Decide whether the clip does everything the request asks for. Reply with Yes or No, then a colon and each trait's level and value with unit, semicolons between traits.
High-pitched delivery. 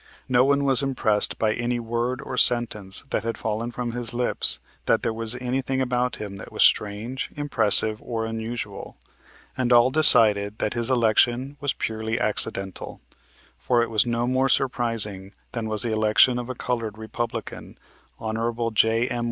No: low, 115 Hz